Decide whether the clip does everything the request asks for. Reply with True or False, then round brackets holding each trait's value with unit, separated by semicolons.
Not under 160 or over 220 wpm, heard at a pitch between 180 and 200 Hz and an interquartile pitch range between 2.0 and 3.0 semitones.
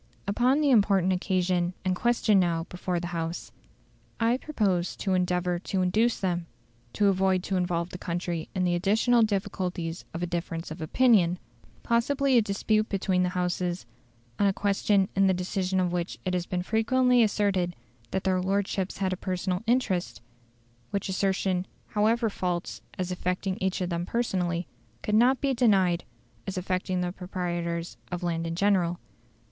True (165 wpm; 185 Hz; 2.5 semitones)